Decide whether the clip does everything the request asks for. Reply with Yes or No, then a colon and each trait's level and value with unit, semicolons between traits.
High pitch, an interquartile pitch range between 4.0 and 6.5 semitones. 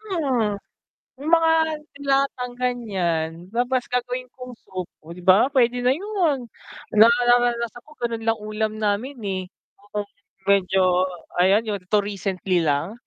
Yes: high, 230 Hz; average, 4.3 semitones